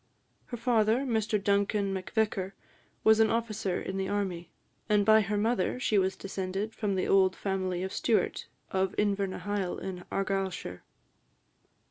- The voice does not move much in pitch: Yes, narrow, 2.3 semitones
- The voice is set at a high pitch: Yes, high, 200 Hz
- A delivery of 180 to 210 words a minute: No, average, 140 wpm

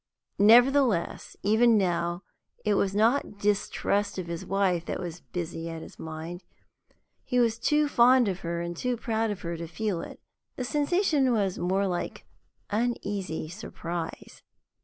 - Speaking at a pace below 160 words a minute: Yes, average, 150 wpm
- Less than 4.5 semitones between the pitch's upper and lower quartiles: No, average, 5.3 semitones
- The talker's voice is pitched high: Yes, high, 200 Hz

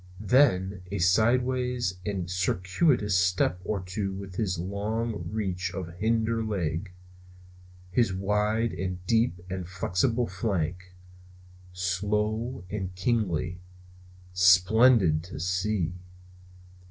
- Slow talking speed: Yes, slow, 100 wpm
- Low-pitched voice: Yes, very low, 95 Hz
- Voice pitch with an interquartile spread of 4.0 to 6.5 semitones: No, average, 3.3 semitones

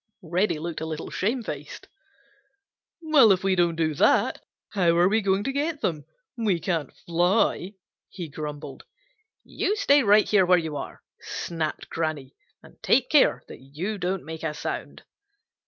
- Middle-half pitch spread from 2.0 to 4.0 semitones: No, average, 4.6 semitones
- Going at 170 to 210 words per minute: No, average, 155 wpm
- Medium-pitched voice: Yes, medium, 175 Hz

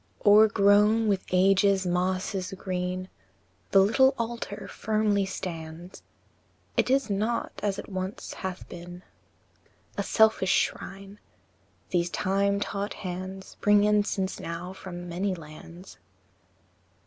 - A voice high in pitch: Yes, high, 195 Hz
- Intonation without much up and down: Yes, narrow, 2.2 semitones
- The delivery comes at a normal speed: No, slow, 115 wpm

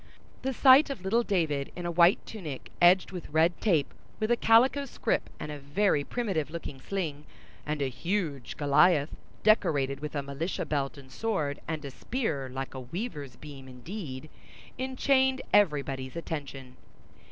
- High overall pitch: No, medium, 155 Hz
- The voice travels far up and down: Yes, wide, 6.7 semitones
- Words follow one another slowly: No, average, 155 wpm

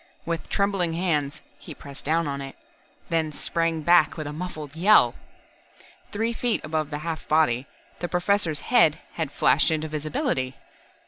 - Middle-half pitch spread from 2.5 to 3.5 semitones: Yes, average, 2.9 semitones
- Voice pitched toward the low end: No, medium, 160 Hz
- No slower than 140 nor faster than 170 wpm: Yes, average, 150 wpm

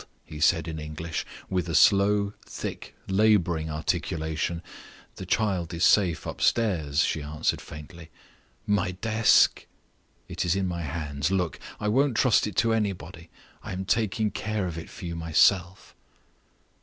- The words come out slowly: No, average, 145 wpm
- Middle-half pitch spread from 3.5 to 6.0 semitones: Yes, average, 4.2 semitones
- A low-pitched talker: Yes, very low, 90 Hz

